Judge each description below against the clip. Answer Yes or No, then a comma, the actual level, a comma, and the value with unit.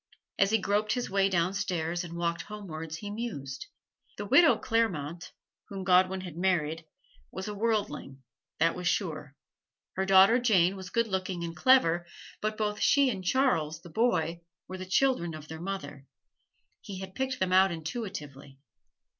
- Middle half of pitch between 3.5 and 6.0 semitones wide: Yes, average, 4.0 semitones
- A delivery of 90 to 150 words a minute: No, average, 160 wpm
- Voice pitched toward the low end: No, medium, 185 Hz